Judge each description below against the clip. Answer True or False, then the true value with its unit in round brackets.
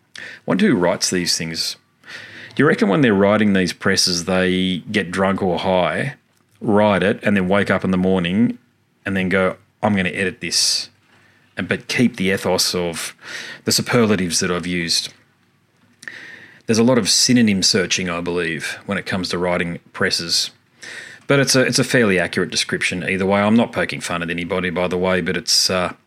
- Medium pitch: False (95 Hz)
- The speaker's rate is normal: True (190 wpm)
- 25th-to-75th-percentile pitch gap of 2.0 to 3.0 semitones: True (2.5 semitones)